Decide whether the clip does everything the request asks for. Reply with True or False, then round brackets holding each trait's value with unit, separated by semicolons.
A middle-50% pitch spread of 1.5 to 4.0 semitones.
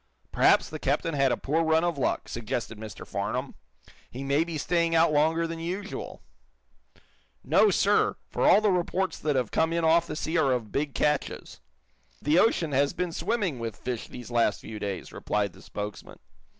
False (5.3 semitones)